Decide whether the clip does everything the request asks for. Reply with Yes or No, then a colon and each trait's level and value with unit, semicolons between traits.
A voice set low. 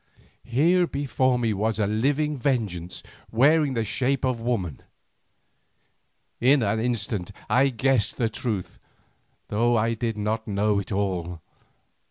Yes: low, 115 Hz